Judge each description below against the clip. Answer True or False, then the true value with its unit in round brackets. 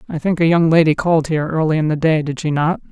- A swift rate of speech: True (290 wpm)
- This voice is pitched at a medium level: True (160 Hz)